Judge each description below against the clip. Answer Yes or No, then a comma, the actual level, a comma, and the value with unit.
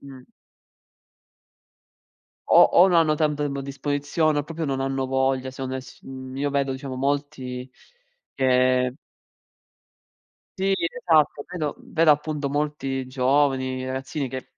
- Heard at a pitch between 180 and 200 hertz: No, low, 135 Hz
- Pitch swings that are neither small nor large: No, narrow, 2.3 semitones